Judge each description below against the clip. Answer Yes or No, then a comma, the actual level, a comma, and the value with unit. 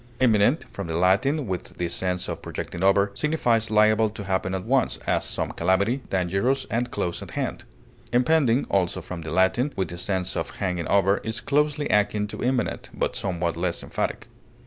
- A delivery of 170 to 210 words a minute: Yes, average, 180 wpm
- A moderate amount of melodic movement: Yes, average, 4.9 semitones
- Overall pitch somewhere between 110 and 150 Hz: No, low, 100 Hz